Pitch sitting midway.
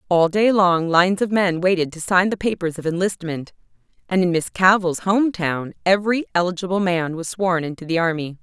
Yes: medium, 180 Hz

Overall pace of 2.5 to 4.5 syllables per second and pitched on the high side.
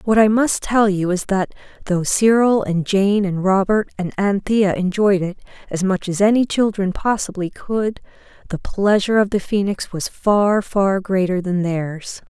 Yes: 4.3 syllables/s; high, 195 Hz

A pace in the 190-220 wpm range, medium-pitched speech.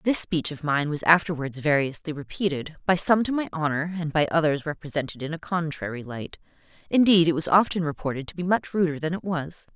Yes: fast, 205 wpm; medium, 160 Hz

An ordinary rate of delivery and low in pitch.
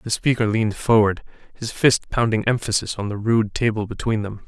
Yes: average, 190 wpm; low, 110 Hz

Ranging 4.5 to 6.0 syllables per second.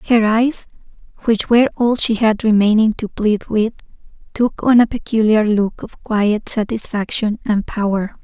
No: 4.3 syllables/s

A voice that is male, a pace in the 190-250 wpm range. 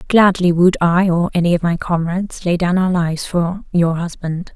No: female; average, 200 wpm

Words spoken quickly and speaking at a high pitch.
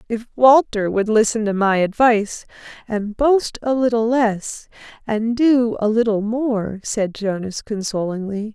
No: average, 140 wpm; high, 220 Hz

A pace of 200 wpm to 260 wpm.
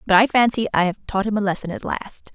No: fast, 280 wpm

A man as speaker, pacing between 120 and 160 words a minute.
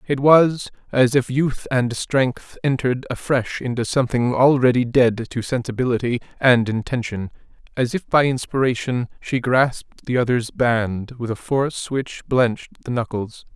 Yes: male; average, 145 wpm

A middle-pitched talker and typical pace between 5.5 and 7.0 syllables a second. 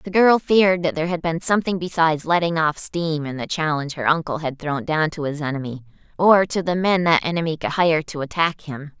Yes: medium, 160 Hz; 5.7 syllables/s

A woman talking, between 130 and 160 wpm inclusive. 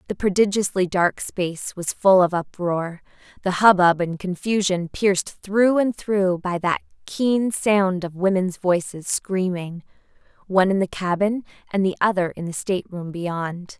Yes: female; average, 150 wpm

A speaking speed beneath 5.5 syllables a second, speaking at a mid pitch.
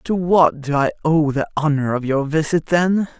Yes: 4.5 syllables/s; medium, 155 Hz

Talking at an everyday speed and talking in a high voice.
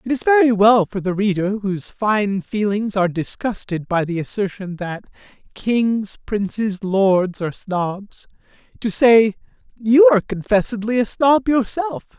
Yes: average, 145 wpm; high, 210 Hz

